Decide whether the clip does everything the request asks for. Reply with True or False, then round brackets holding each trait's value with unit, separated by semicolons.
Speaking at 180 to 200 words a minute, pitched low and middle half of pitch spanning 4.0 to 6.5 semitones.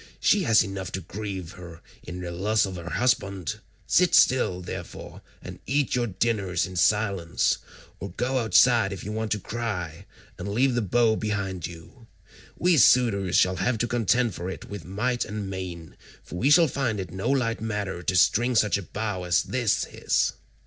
True (185 wpm; 105 Hz; 4.5 semitones)